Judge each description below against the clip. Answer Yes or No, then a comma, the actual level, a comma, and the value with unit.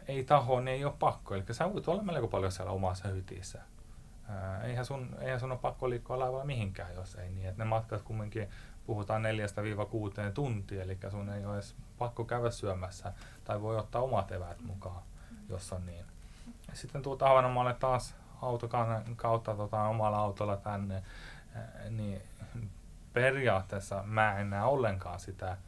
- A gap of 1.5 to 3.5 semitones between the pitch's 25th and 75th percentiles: No, average, 3.9 semitones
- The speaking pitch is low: Yes, low, 110 Hz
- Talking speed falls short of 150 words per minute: No, fast, 155 wpm